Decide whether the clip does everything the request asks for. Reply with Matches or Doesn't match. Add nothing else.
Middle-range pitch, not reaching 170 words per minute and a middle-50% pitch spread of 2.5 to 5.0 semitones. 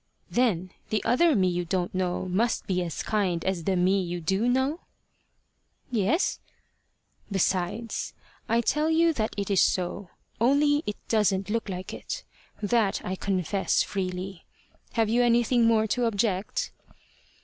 Doesn't match